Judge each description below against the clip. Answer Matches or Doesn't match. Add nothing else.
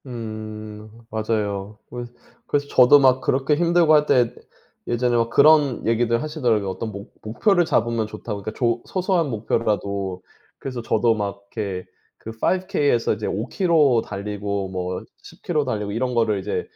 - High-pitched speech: Doesn't match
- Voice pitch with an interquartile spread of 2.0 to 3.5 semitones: Doesn't match